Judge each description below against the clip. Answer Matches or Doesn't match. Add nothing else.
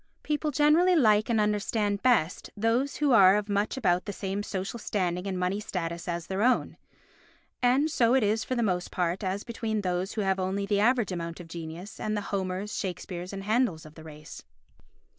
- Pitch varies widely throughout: Doesn't match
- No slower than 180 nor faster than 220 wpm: Matches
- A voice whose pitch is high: Matches